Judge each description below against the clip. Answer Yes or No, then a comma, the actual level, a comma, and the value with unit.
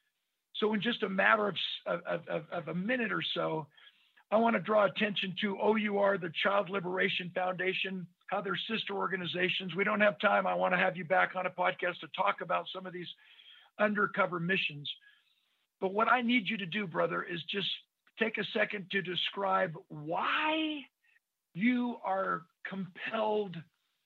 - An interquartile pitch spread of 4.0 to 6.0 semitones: No, average, 2.8 semitones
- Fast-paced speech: No, average, 165 wpm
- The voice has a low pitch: No, high, 195 Hz